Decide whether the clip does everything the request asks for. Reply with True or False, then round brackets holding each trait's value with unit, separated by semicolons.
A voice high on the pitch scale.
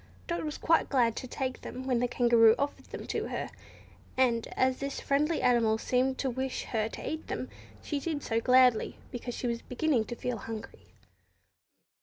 True (250 Hz)